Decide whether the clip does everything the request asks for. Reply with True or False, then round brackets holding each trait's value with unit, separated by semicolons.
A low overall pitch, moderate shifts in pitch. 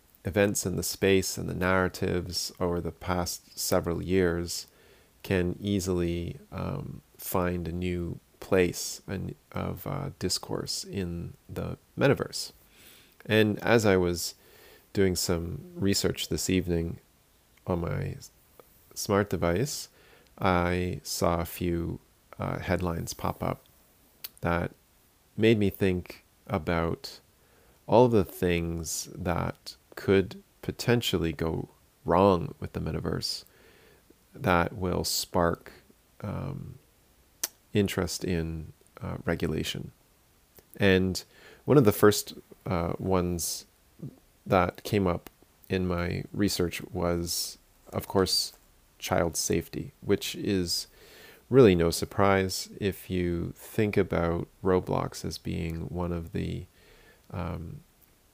False (90 Hz; 2.3 semitones)